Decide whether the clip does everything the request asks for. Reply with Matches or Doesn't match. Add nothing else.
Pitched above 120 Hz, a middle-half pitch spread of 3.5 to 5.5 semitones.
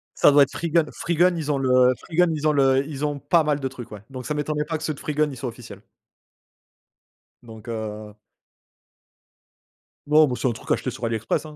Matches